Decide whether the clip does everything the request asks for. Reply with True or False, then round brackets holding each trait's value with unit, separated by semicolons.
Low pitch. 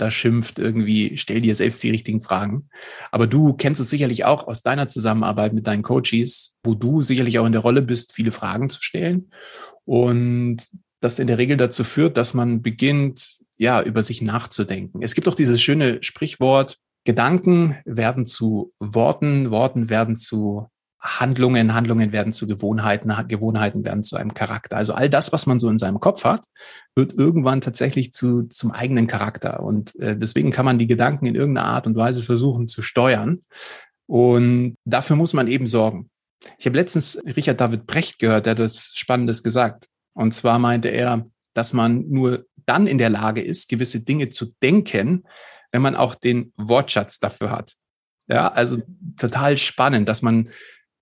True (120 Hz)